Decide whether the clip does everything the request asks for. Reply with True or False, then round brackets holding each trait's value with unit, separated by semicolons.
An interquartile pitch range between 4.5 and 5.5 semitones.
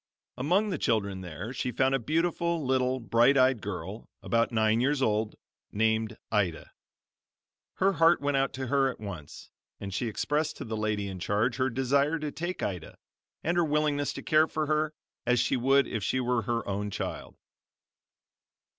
True (5.2 semitones)